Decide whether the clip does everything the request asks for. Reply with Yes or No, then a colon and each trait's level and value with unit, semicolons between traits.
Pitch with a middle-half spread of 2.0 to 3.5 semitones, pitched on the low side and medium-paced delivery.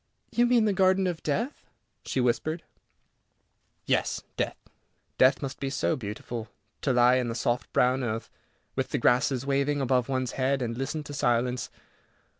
Yes: average, 3.1 semitones; low, 130 Hz; average, 160 wpm